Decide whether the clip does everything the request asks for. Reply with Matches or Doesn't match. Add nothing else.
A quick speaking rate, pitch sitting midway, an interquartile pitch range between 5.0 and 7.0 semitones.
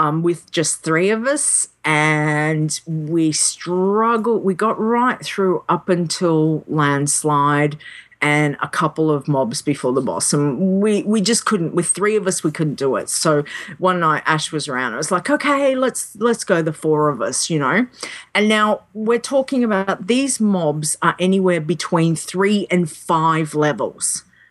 Doesn't match